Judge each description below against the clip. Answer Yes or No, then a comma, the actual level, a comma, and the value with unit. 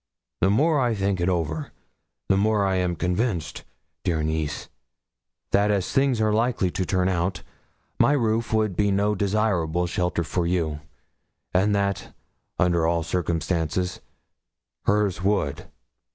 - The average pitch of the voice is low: Yes, very low, 95 Hz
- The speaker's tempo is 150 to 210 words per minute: No, slow, 135 wpm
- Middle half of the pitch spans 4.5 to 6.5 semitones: No, average, 3.5 semitones